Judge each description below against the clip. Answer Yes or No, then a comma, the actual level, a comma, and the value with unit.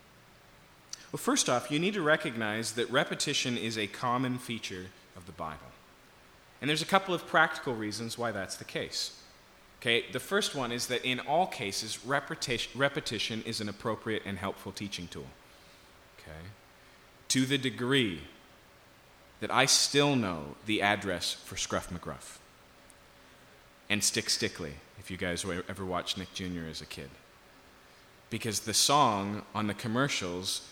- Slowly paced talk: No, average, 150 wpm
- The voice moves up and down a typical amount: No, wide, 5.8 semitones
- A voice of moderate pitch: No, low, 105 Hz